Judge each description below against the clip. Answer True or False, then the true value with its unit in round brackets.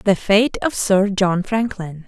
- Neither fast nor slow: True (175 wpm)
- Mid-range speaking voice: False (195 Hz)